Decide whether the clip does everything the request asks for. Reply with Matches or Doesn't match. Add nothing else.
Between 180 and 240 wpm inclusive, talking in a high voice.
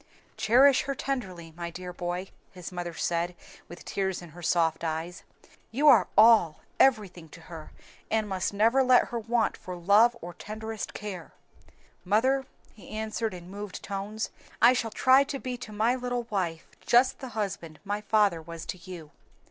Doesn't match